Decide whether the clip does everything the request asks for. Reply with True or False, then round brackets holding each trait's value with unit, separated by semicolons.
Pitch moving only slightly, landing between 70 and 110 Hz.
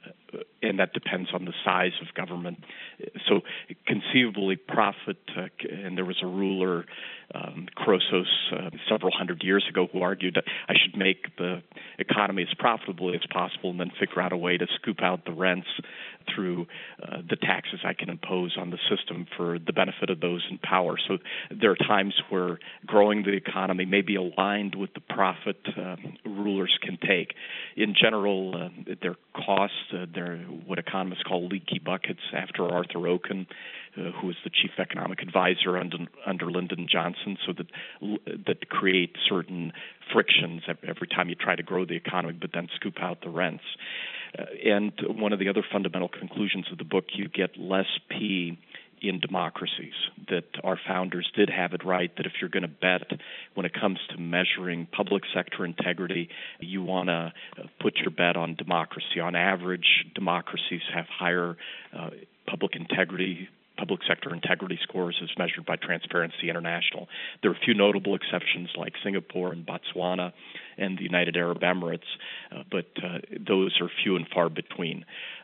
True (1.5 semitones; 90 Hz)